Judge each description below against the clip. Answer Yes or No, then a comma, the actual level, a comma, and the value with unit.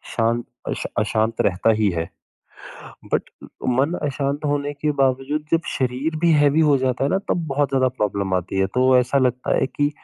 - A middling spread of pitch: Yes, average, 3.5 semitones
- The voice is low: Yes, low, 130 Hz